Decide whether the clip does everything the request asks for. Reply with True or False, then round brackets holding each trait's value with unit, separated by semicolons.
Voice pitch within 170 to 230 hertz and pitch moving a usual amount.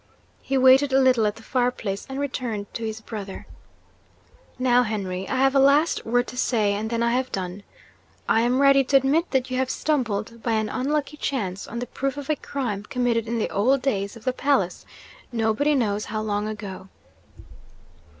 False (240 Hz; 4.0 semitones)